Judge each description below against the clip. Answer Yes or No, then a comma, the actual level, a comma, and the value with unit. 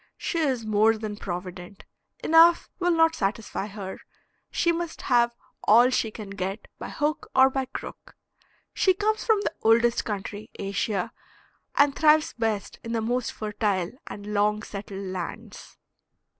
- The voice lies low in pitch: No, high, 225 Hz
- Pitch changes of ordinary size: No, wide, 5.7 semitones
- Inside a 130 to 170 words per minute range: Yes, average, 145 wpm